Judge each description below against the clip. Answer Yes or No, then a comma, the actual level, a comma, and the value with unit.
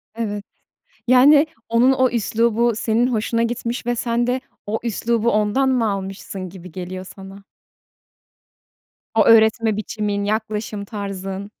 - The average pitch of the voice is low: No, high, 220 Hz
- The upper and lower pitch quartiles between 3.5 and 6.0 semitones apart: No, average, 2.7 semitones